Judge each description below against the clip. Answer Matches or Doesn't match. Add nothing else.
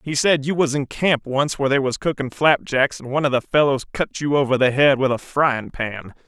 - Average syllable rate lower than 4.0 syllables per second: Doesn't match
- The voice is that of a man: Matches